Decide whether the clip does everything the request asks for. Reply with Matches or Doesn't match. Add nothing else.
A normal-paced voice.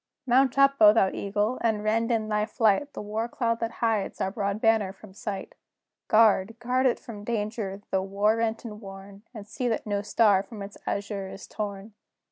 Matches